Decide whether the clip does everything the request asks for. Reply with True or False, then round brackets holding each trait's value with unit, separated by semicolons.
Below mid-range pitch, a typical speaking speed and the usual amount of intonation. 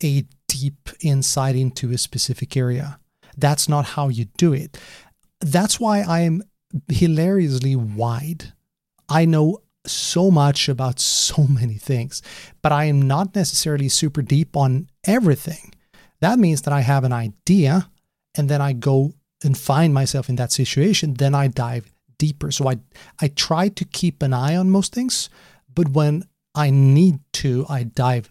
False (145 Hz; 160 wpm; 3.8 semitones)